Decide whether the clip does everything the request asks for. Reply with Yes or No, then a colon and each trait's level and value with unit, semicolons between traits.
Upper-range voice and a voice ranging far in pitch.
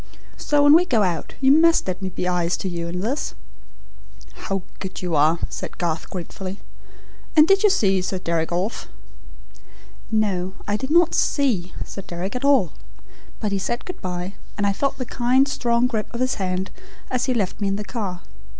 Yes: high, 200 Hz; wide, 5.9 semitones